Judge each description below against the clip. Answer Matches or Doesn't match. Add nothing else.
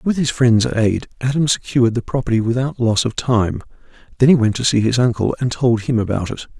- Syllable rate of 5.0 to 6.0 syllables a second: Matches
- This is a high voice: Doesn't match